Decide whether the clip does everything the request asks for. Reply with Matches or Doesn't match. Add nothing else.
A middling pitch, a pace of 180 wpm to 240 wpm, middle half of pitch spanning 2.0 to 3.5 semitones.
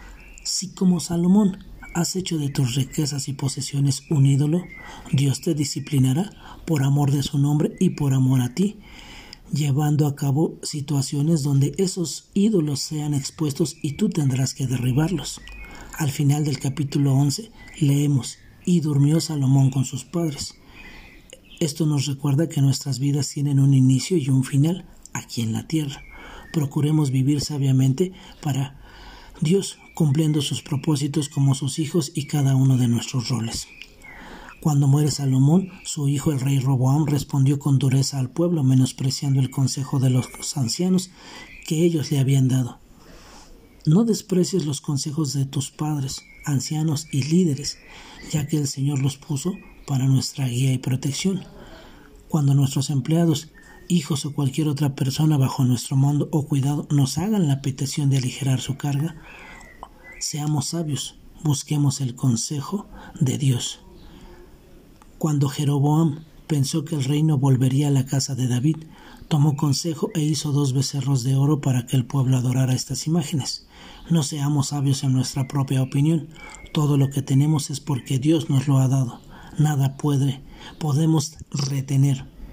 Doesn't match